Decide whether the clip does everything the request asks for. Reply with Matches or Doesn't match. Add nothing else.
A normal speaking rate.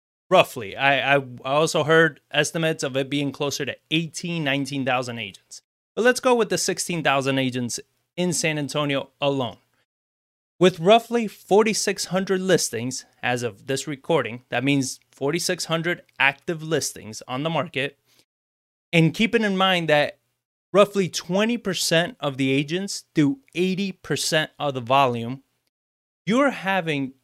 Doesn't match